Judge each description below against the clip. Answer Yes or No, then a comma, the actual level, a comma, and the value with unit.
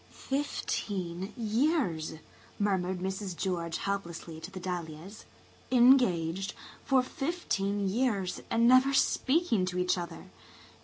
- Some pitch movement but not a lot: No, wide, 5.7 semitones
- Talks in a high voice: Yes, high, 195 Hz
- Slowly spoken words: Yes, slow, 105 wpm